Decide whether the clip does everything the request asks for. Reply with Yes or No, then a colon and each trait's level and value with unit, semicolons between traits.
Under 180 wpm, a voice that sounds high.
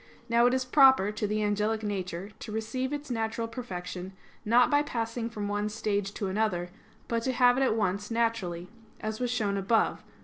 No: average, 195 wpm; high, 220 Hz